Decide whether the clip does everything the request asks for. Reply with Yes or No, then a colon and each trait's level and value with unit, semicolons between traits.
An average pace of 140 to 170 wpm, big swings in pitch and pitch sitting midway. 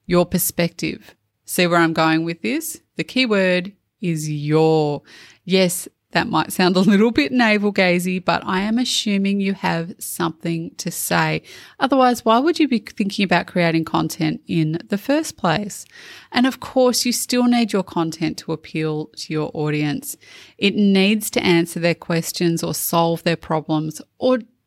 Yes: average, 160 wpm; wide, 5.8 semitones; medium, 180 Hz